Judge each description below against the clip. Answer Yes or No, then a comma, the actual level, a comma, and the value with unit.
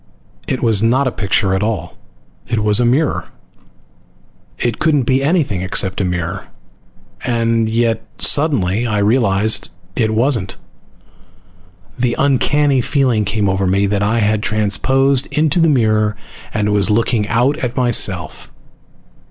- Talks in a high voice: No, low, 115 Hz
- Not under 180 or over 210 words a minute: No, slow, 135 wpm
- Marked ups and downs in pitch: No, average, 4.0 semitones